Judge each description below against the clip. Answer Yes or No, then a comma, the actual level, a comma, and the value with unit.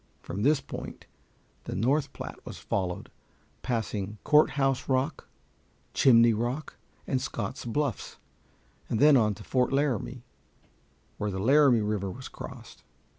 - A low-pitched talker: Yes, low, 125 Hz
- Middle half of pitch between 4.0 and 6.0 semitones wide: Yes, average, 4.5 semitones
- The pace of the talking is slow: Yes, slow, 125 wpm